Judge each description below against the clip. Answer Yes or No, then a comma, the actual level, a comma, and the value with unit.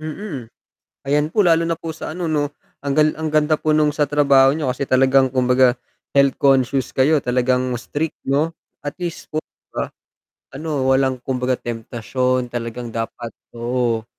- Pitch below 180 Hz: Yes, low, 135 Hz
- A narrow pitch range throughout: No, average, 3.3 semitones